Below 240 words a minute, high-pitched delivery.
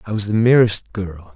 No: fast, 220 wpm; low, 105 Hz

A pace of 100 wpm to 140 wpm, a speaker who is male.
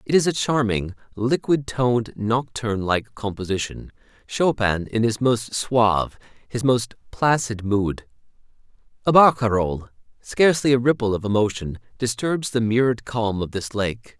Yes: slow, 135 wpm; male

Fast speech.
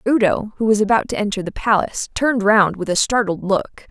Yes: fast, 215 wpm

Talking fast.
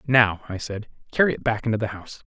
Yes: fast, 235 wpm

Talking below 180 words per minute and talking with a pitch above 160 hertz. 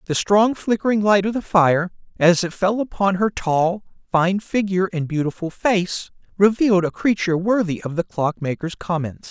Yes: average, 170 wpm; medium, 185 Hz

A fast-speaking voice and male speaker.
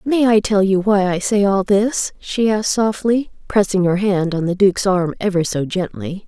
No: fast, 210 wpm; female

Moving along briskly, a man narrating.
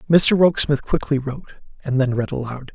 No: average, 175 wpm; male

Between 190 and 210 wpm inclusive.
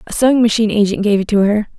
No: fast, 270 wpm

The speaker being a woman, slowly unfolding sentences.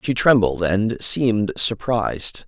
No: male; slow, 120 wpm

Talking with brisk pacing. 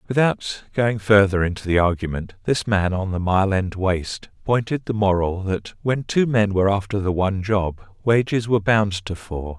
No: average, 190 wpm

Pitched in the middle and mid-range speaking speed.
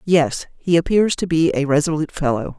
Yes: medium, 160 Hz; average, 185 wpm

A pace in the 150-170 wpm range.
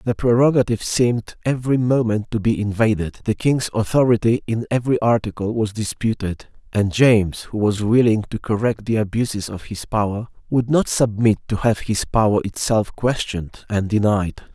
Yes: average, 160 wpm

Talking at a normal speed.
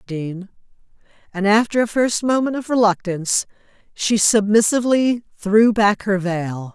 No: slow, 125 wpm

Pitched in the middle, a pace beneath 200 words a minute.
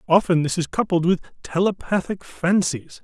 Yes: medium, 175 Hz; average, 140 wpm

